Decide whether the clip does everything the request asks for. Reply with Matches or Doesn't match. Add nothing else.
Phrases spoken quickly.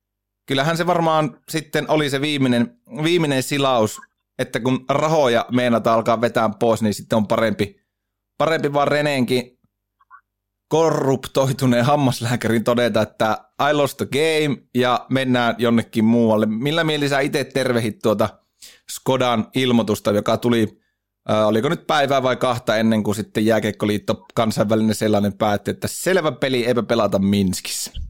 Doesn't match